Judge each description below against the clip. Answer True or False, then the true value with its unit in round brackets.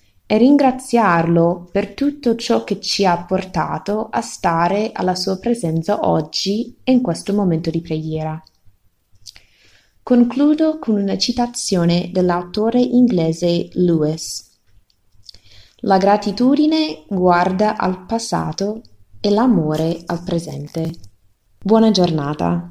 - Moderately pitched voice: True (175 Hz)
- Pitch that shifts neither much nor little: False (5.9 semitones)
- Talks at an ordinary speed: False (105 wpm)